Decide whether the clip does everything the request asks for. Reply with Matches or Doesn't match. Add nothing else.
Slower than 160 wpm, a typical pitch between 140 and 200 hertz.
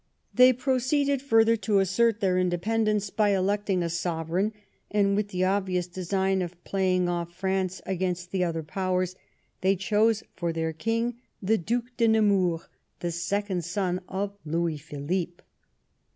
Matches